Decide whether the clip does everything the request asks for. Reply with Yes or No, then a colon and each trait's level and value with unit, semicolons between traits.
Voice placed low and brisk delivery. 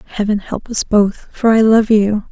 No: high, 210 Hz; fast, 210 wpm